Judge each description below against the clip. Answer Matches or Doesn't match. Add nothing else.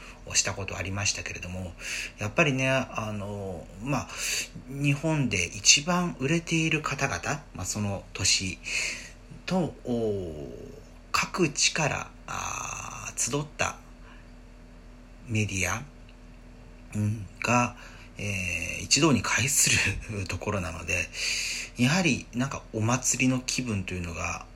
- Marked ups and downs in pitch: Matches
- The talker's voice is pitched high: Doesn't match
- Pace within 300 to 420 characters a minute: Doesn't match